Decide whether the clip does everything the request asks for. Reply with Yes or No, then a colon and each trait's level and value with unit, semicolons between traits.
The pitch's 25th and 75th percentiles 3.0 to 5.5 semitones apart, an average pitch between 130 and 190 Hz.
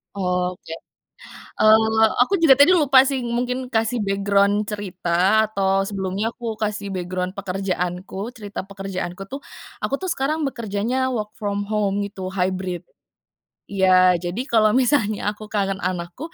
No: average, 3.4 semitones; high, 205 Hz